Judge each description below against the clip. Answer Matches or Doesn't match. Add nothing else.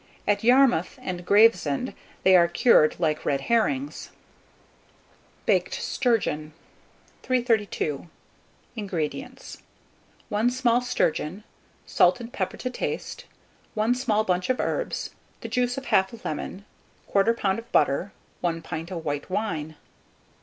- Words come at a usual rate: Doesn't match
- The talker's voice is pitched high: Matches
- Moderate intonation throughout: Doesn't match